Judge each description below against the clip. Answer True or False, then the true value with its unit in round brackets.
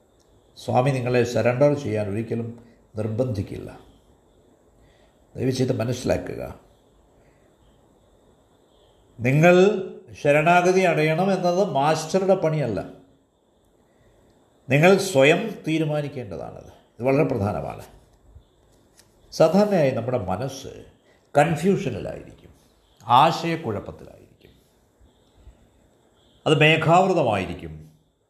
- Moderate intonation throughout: False (6.7 semitones)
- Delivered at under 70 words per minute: True (60 wpm)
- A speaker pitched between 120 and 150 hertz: True (135 Hz)